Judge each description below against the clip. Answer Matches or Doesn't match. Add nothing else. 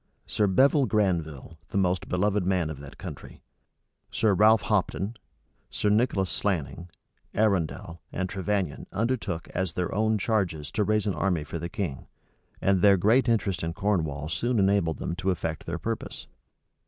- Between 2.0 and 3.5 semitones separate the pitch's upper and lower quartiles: Doesn't match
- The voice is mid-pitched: Doesn't match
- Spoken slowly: Doesn't match